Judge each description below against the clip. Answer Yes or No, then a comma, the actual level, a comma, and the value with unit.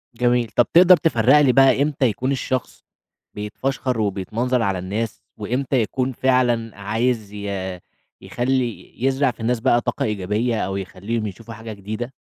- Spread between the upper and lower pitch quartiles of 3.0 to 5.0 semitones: Yes, average, 3.6 semitones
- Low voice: Yes, low, 115 Hz